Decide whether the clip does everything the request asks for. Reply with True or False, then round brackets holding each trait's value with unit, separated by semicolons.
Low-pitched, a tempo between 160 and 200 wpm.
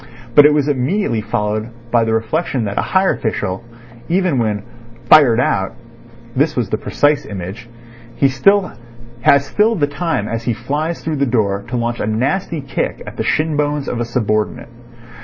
True (125 Hz; 170 wpm)